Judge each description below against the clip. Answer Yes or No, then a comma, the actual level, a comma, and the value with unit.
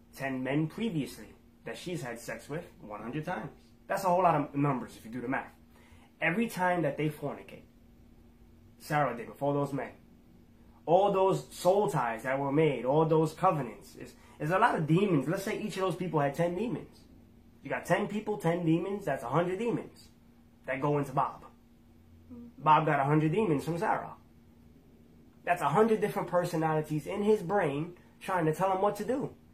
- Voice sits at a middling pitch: Yes, medium, 160 Hz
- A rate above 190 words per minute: No, average, 185 wpm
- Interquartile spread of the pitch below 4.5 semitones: No, average, 5.3 semitones